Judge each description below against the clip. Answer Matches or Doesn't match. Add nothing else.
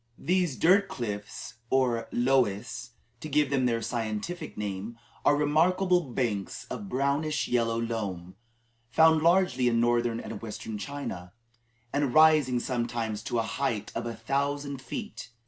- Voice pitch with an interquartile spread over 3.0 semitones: Matches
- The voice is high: Doesn't match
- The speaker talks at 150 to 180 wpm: Doesn't match